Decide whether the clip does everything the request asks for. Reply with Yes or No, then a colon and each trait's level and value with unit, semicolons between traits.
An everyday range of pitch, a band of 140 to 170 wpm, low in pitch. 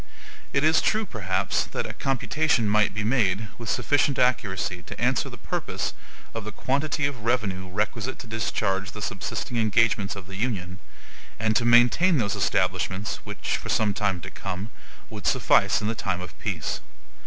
Yes: average, 4.0 semitones; average, 165 wpm; low, 110 Hz